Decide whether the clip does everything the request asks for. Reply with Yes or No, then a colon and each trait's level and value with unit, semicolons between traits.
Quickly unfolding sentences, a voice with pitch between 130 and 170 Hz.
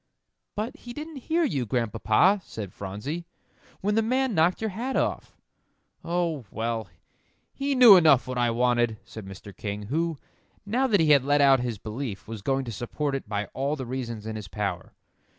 No: average, 185 wpm; low, 135 Hz